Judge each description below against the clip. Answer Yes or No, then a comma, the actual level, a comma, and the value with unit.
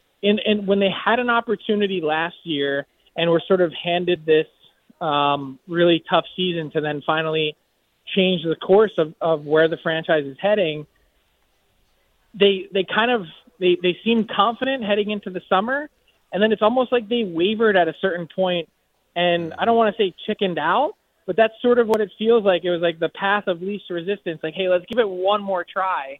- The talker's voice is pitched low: No, medium, 185 Hz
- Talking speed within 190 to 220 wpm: Yes, average, 200 wpm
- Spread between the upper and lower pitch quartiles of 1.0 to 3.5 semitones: No, average, 4.3 semitones